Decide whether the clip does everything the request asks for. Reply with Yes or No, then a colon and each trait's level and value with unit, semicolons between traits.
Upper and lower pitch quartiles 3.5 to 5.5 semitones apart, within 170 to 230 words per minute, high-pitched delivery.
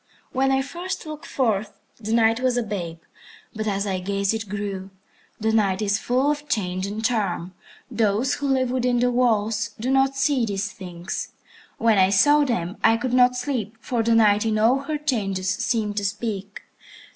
Yes: average, 4.0 semitones; average, 185 wpm; high, 220 Hz